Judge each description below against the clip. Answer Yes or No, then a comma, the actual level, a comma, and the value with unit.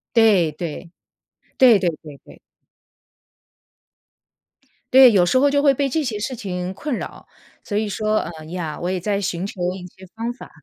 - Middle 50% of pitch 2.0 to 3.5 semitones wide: No, average, 5.3 semitones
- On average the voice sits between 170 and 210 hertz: Yes, high, 205 Hz